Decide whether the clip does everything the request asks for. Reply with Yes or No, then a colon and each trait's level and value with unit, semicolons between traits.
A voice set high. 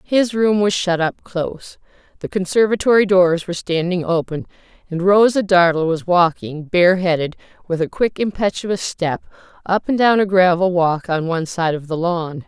No: medium, 180 Hz